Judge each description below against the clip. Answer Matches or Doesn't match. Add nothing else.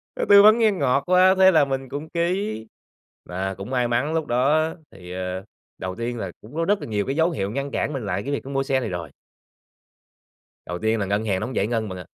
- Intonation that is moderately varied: Doesn't match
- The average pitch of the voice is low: Matches